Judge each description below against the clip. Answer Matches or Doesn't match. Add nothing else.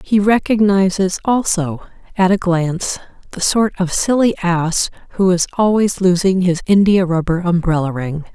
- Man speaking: Doesn't match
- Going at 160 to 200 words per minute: Doesn't match